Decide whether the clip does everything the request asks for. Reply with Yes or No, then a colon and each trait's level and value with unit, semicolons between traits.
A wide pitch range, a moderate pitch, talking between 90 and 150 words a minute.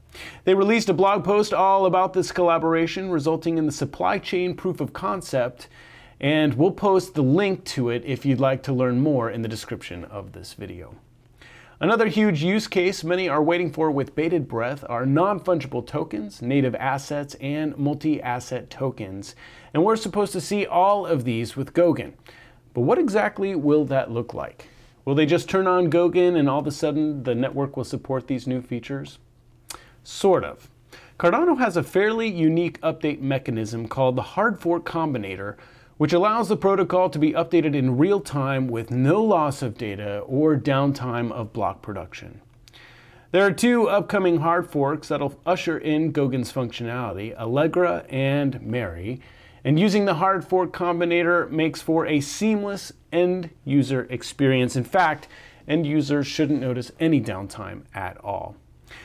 No: wide, 5.9 semitones; medium, 145 Hz; average, 165 wpm